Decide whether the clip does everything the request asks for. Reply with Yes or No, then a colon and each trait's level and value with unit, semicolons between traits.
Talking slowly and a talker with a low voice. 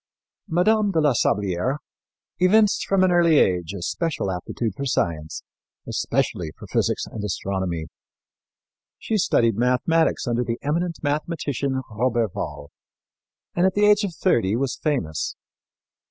Yes: slow, 130 wpm; low, 130 Hz